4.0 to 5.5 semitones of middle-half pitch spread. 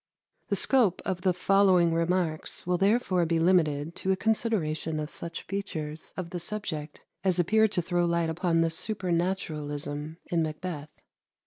No: average, 3.0 semitones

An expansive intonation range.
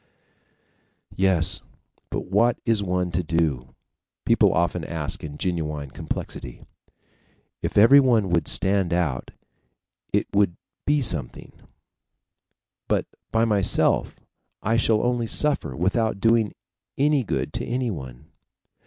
Yes: wide, 5.7 semitones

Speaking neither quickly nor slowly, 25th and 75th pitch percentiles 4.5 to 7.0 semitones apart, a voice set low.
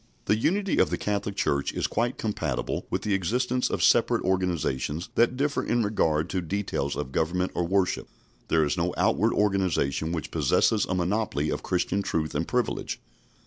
Yes: average, 175 wpm; average, 4.9 semitones; very low, 95 Hz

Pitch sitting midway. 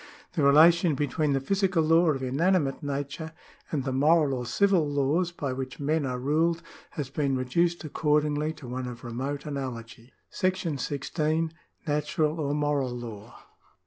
Yes: medium, 145 Hz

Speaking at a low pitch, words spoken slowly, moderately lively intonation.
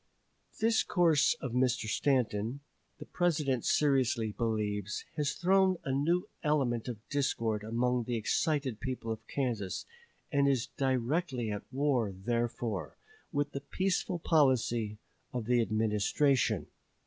Yes: low, 125 Hz; slow, 125 wpm; average, 4.3 semitones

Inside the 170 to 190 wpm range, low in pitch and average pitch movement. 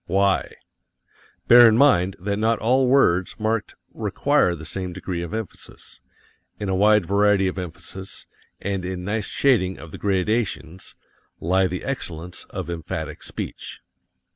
No: average, 140 wpm; very low, 95 Hz; average, 3.2 semitones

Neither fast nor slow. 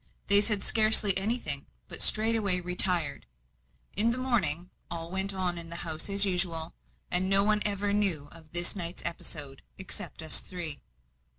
Yes: average, 160 wpm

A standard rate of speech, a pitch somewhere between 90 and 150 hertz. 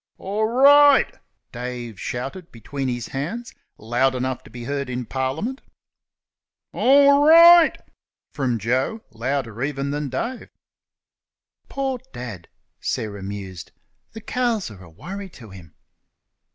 No: slow, 120 wpm; low, 135 Hz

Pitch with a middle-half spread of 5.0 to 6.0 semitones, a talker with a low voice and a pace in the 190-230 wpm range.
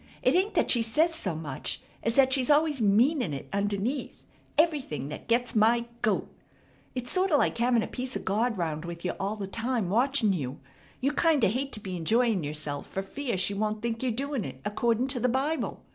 No: wide, 5.4 semitones; high, 230 Hz; fast, 205 wpm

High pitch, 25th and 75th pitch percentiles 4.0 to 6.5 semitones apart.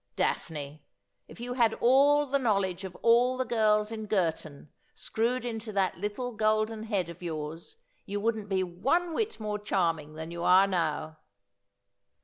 Yes: high, 210 Hz; average, 5.3 semitones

